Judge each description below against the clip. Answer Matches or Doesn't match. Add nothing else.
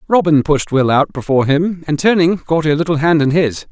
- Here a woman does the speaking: Doesn't match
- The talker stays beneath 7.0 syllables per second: Matches